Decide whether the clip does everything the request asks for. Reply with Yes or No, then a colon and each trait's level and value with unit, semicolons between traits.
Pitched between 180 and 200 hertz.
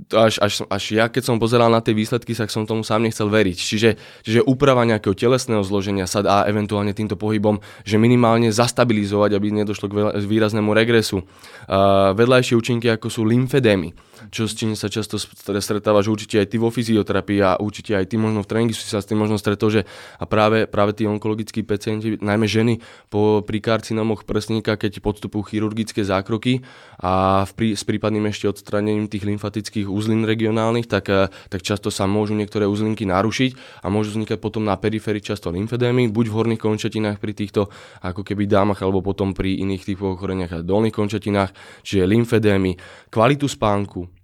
No: low, 105 Hz